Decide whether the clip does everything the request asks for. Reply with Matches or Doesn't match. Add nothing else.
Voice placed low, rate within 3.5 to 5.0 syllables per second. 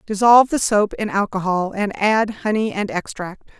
Doesn't match